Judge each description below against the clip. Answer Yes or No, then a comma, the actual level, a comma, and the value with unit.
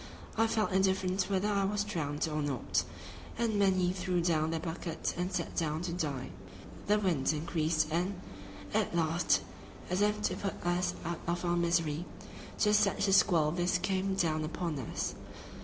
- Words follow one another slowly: No, average, 175 wpm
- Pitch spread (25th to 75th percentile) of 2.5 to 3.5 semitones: Yes, average, 3.2 semitones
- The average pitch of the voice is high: No, medium, 175 Hz